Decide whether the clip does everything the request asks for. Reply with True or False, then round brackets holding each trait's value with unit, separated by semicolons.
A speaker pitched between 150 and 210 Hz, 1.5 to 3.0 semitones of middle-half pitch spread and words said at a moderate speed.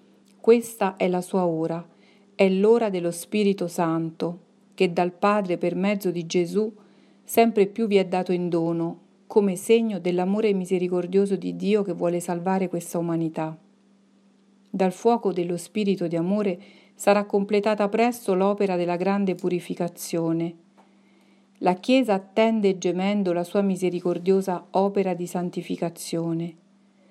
True (190 Hz; 2.6 semitones; 130 wpm)